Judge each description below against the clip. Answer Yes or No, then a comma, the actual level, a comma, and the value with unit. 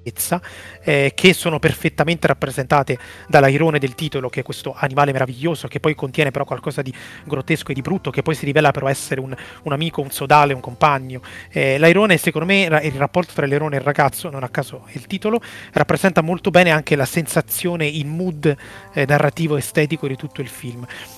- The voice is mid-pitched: Yes, medium, 145 Hz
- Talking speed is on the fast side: Yes, fast, 190 wpm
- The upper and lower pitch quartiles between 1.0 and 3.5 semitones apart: Yes, average, 2.9 semitones